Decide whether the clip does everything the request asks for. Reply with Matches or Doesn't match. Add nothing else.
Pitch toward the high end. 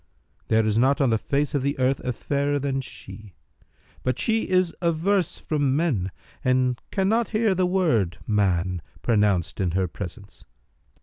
Doesn't match